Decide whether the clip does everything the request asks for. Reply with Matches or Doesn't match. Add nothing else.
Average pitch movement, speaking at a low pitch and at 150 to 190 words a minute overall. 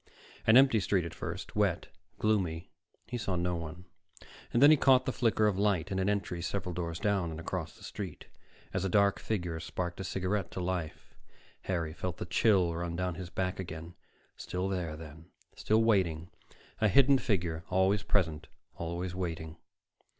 Matches